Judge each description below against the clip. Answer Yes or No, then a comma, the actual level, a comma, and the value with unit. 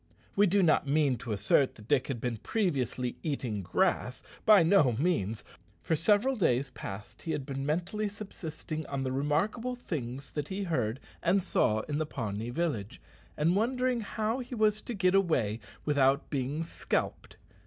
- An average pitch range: No, wide, 7.6 semitones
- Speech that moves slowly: No, average, 165 wpm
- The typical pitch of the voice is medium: Yes, medium, 150 Hz